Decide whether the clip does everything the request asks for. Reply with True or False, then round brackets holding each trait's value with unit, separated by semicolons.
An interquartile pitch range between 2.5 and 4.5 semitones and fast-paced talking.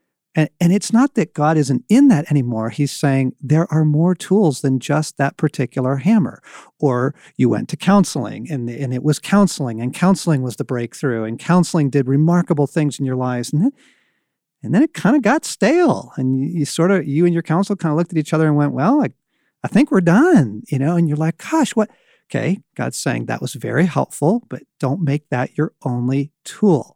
False (5.4 semitones; 220 wpm)